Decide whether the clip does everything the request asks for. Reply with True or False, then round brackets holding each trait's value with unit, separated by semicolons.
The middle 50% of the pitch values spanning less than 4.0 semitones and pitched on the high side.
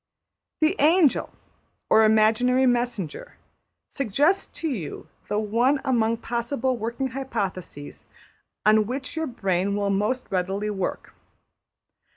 False (4.3 semitones; 230 Hz)